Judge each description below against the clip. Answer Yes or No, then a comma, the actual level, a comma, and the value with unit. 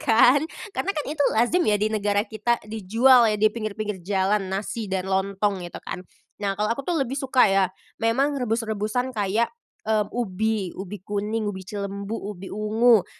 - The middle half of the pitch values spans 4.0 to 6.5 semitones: No, average, 2.7 semitones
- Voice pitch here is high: Yes, high, 215 Hz